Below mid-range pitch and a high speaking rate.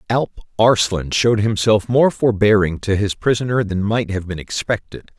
No: low, 105 Hz; average, 160 wpm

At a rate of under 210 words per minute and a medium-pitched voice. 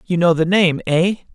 No: fast, 225 wpm; medium, 175 Hz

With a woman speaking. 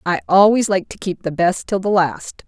Yes: female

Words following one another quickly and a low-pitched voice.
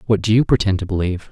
Yes: fast, 275 wpm; low, 100 Hz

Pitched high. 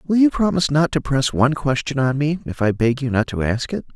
No: medium, 140 Hz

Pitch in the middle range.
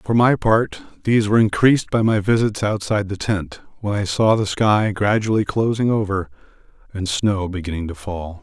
No: low, 105 Hz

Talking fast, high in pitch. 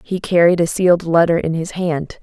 No: fast, 215 wpm; medium, 170 Hz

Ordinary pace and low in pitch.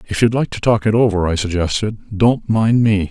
No: fast, 230 wpm; low, 105 Hz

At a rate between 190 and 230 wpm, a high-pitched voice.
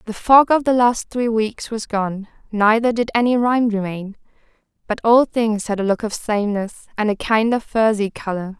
Yes: average, 195 wpm; high, 220 Hz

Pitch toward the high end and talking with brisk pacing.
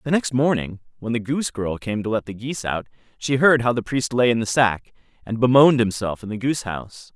No: low, 120 Hz; fast, 245 wpm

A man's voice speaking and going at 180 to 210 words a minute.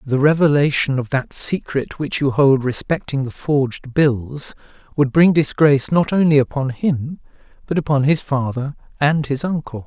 No: male; average, 160 wpm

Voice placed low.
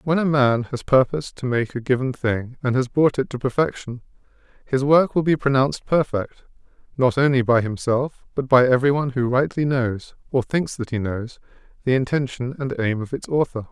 Yes: low, 130 Hz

